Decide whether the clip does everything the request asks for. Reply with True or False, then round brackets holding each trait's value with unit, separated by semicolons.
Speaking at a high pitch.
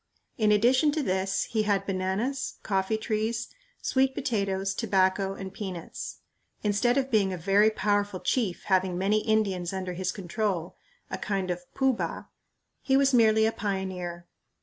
True (200 Hz)